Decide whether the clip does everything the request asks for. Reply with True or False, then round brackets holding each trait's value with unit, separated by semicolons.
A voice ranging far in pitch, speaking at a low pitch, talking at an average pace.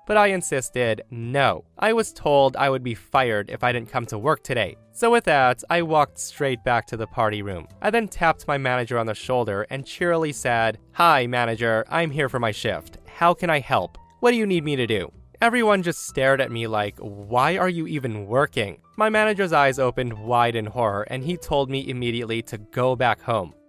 False (6.1 semitones; 130 Hz; 215 wpm)